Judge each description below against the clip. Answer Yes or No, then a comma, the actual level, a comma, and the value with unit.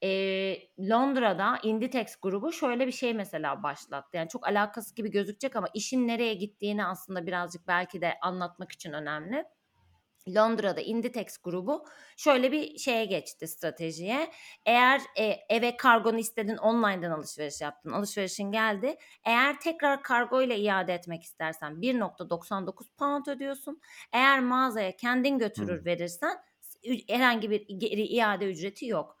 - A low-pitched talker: No, high, 215 Hz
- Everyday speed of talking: Yes, average, 125 wpm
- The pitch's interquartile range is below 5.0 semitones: No, wide, 5.4 semitones